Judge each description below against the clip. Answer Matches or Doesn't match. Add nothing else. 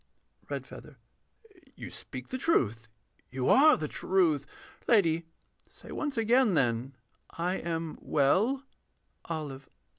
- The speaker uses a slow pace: Matches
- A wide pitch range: Matches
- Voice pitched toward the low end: Doesn't match